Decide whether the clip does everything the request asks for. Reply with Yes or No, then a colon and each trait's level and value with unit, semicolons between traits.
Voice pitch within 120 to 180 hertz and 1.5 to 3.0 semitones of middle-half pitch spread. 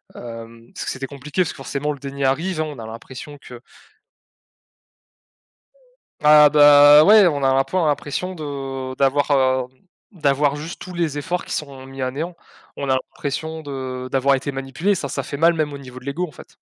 Yes: medium, 140 Hz; narrow, 2.4 semitones